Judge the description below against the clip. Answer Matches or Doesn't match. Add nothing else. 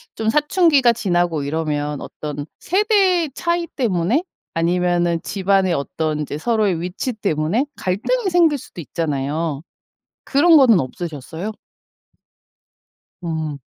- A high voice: Doesn't match